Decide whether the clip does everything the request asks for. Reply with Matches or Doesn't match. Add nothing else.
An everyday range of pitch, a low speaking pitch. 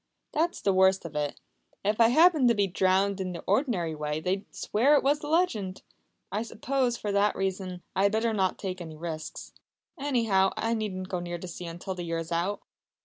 Doesn't match